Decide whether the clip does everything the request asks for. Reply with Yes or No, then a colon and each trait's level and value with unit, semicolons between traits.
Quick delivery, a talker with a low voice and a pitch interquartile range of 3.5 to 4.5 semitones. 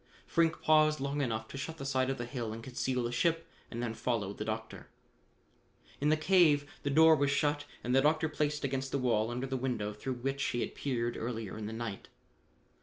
Yes: fast, 215 wpm; low, 130 Hz; average, 3.9 semitones